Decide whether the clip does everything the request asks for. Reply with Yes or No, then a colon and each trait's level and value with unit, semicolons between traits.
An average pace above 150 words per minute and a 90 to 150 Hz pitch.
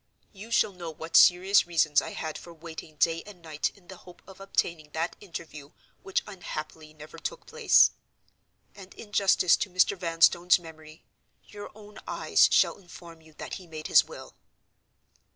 No: average, 170 wpm; medium, 170 Hz